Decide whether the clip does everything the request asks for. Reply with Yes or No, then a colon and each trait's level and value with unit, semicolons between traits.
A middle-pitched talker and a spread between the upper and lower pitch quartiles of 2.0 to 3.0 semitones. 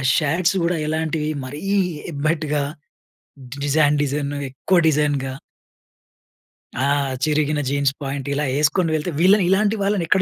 Yes: medium, 150 Hz; average, 2.7 semitones